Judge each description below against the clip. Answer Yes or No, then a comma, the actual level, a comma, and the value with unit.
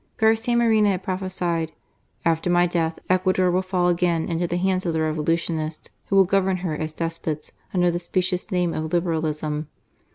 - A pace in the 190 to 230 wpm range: No, average, 170 wpm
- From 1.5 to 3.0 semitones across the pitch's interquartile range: Yes, narrow, 2.4 semitones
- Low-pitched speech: No, medium, 175 Hz